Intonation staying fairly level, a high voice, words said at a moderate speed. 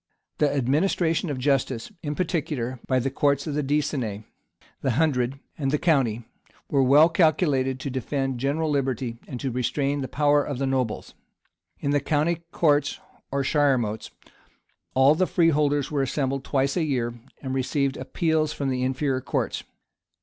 No: narrow, 2.3 semitones; medium, 140 Hz; average, 155 wpm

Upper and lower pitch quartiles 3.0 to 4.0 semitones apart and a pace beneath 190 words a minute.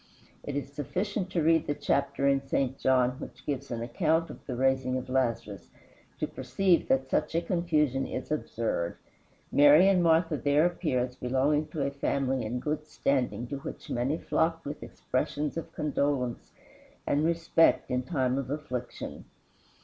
Yes: average, 3.5 semitones; average, 165 wpm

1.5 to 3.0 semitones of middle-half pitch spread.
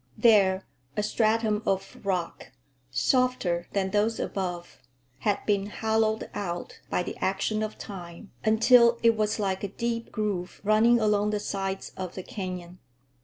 Yes: narrow, 2.6 semitones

